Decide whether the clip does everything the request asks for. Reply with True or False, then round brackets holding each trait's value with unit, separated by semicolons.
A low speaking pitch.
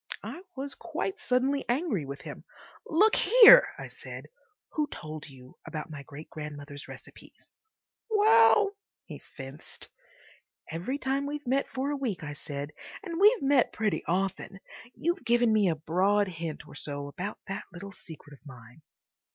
False (200 Hz)